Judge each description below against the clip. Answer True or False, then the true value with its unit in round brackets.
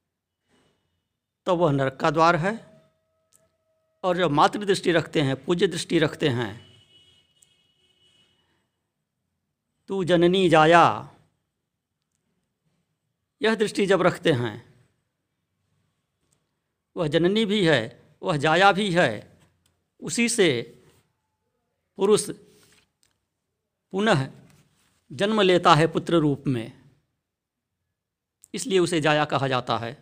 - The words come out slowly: True (95 wpm)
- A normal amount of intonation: False (7.0 semitones)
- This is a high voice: False (155 Hz)